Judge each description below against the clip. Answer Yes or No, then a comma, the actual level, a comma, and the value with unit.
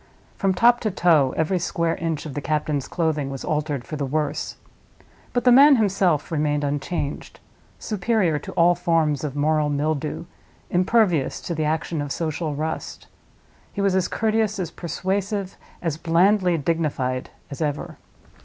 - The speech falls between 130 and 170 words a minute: Yes, average, 150 wpm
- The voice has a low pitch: No, medium, 165 Hz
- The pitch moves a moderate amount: Yes, average, 4.2 semitones